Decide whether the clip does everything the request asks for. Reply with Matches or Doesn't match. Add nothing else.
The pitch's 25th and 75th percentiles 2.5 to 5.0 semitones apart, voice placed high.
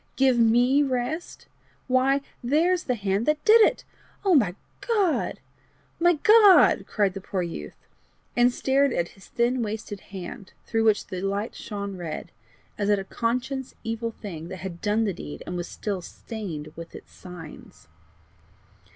Doesn't match